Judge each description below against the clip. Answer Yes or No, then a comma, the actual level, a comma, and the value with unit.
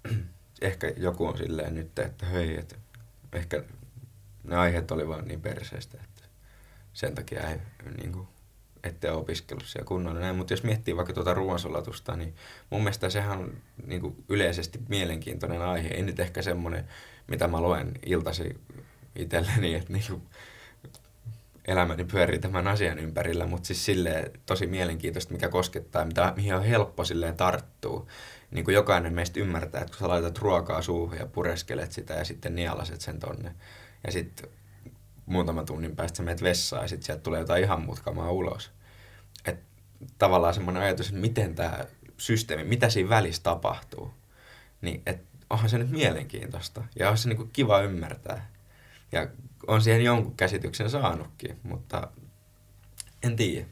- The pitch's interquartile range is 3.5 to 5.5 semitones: Yes, average, 4.3 semitones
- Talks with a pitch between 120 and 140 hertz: No, low, 100 Hz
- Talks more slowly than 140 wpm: No, fast, 155 wpm